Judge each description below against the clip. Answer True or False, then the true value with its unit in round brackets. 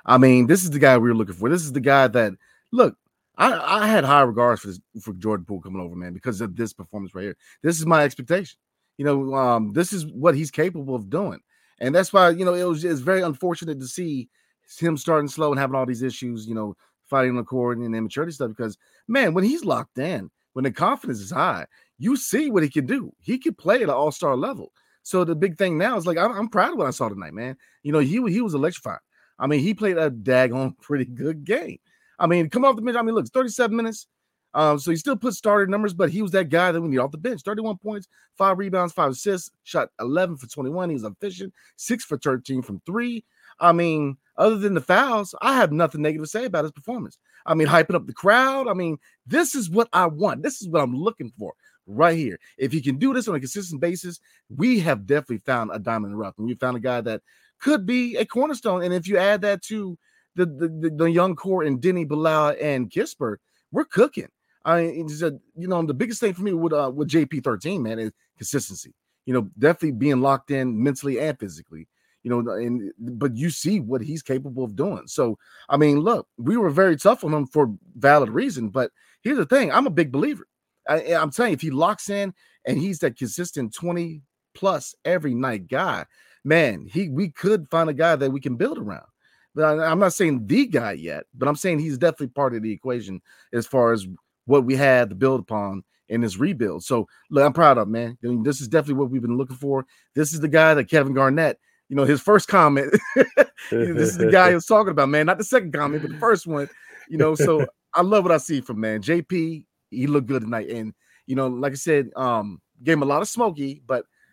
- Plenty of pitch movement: True (5.9 semitones)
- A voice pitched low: False (155 Hz)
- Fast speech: True (240 wpm)